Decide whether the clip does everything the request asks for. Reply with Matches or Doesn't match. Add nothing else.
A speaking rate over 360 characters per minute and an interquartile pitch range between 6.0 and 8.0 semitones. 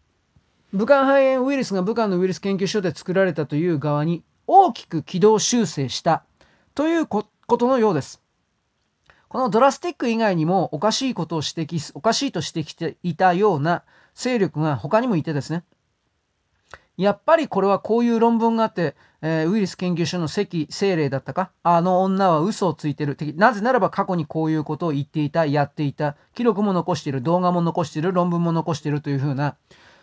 Doesn't match